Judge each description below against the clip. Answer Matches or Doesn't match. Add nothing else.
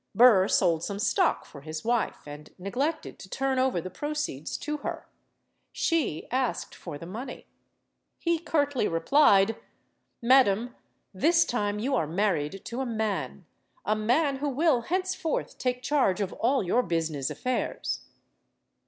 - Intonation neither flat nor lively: Doesn't match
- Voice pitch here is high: Matches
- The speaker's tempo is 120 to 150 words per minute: Matches